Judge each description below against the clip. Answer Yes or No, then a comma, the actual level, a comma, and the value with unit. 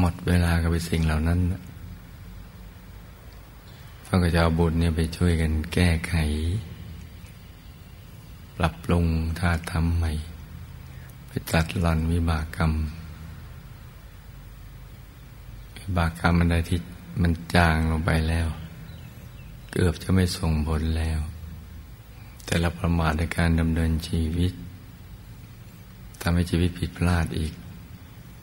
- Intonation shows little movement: Yes, narrow, 2.0 semitones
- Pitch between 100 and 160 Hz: No, very low, 85 Hz